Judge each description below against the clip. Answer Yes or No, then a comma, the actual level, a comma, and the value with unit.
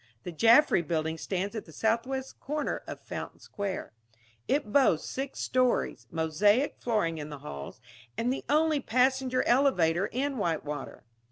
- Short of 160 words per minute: Yes, average, 145 wpm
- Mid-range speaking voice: No, high, 220 Hz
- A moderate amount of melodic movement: No, wide, 8.3 semitones